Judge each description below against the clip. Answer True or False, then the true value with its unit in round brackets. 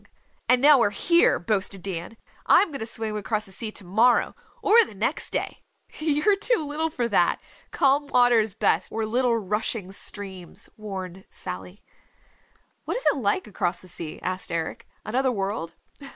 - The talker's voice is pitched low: False (215 Hz)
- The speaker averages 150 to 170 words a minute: True (165 wpm)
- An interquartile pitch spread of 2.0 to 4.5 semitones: False (5.4 semitones)